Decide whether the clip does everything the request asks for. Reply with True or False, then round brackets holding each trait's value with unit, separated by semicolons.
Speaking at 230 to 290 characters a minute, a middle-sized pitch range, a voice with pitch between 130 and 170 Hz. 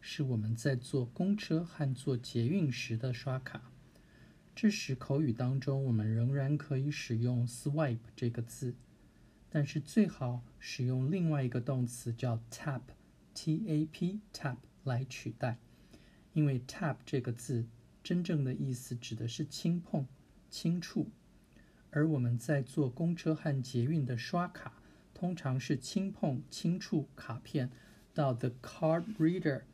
True (240 characters per minute; 4.3 semitones; 135 Hz)